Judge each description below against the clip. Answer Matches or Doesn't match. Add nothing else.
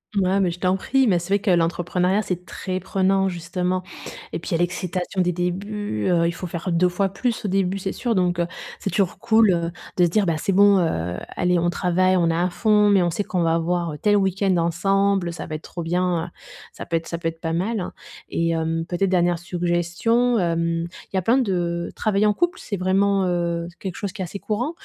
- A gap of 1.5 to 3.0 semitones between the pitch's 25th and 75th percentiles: Matches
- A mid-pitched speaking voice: Matches